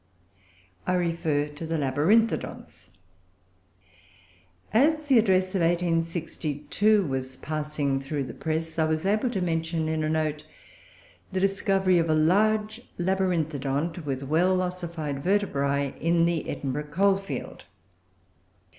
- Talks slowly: Yes, slow, 120 wpm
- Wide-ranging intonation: No, average, 4.0 semitones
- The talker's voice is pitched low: No, medium, 165 Hz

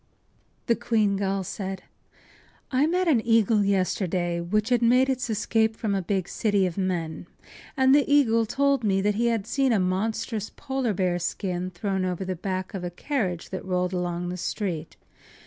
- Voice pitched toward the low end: No, high, 200 Hz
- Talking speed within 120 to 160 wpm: No, average, 180 wpm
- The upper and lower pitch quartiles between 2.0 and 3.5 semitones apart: No, average, 4.0 semitones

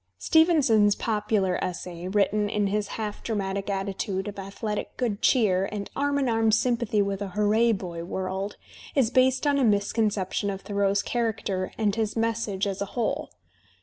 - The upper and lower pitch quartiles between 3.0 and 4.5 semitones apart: No, narrow, 2.6 semitones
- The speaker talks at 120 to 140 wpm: No, average, 160 wpm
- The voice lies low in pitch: No, high, 205 Hz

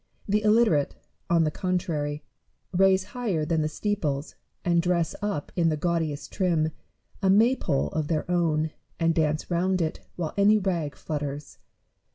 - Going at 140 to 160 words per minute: Yes, average, 150 wpm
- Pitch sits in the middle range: Yes, medium, 170 Hz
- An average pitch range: Yes, average, 3.7 semitones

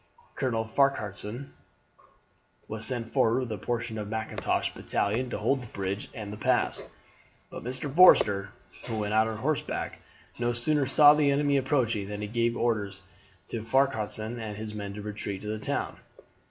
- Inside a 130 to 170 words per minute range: Yes, average, 165 wpm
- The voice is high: No, low, 110 Hz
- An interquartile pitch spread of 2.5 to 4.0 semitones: Yes, average, 3.5 semitones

